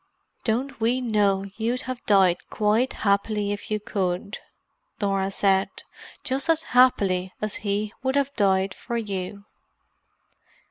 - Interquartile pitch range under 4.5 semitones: Yes, average, 3.5 semitones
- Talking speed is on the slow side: Yes, slow, 130 wpm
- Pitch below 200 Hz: No, high, 210 Hz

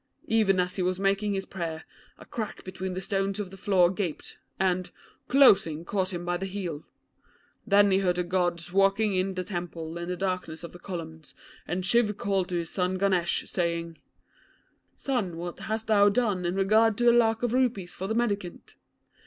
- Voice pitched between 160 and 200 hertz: Yes, high, 190 Hz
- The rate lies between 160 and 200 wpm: Yes, average, 190 wpm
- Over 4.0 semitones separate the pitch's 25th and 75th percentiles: No, narrow, 2.5 semitones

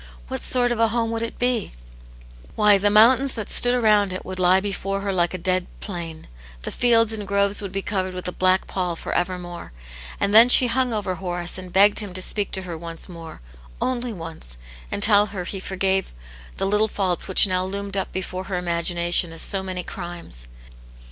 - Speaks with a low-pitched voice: No, high, 190 Hz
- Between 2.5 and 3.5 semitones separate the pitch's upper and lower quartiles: Yes, average, 2.9 semitones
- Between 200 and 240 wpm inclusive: Yes, fast, 205 wpm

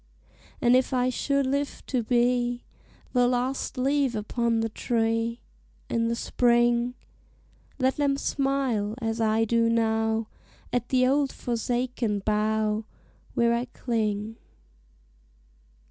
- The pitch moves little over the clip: Yes, narrow, 2.1 semitones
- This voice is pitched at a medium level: No, high, 240 Hz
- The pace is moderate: No, slow, 115 wpm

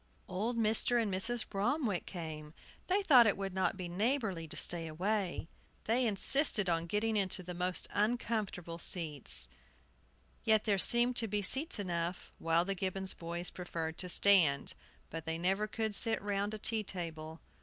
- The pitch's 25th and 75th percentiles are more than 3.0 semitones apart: Yes, average, 4.2 semitones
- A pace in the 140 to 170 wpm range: Yes, average, 165 wpm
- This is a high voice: Yes, high, 195 Hz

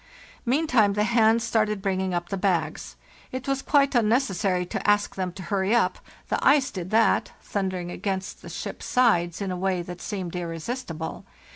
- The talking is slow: No, average, 165 wpm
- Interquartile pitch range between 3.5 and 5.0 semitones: Yes, average, 4.3 semitones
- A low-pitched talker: No, high, 195 Hz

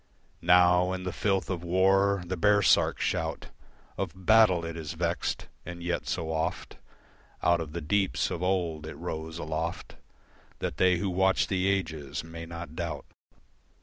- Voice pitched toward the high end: No, very low, 85 Hz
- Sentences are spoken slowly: No, average, 155 wpm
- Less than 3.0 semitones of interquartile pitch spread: Yes, narrow, 2.4 semitones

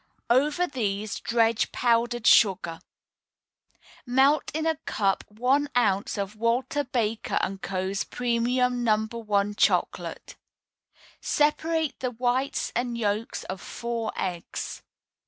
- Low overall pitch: No, high, 235 Hz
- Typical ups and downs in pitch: Yes, average, 3.6 semitones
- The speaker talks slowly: Yes, slow, 110 wpm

